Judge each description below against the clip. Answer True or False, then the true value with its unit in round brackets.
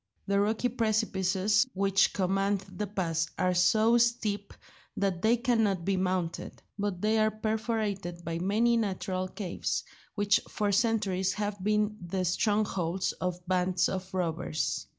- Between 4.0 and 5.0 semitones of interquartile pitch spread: False (2.7 semitones)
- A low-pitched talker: False (200 Hz)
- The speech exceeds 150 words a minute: False (135 wpm)